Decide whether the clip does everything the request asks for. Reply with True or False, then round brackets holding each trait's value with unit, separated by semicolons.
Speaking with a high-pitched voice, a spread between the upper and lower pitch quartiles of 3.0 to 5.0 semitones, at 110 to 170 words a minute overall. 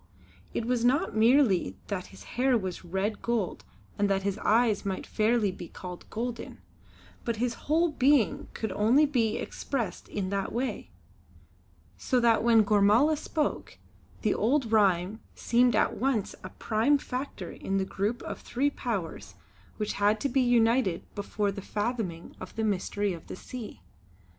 True (220 Hz; 3.8 semitones; 160 wpm)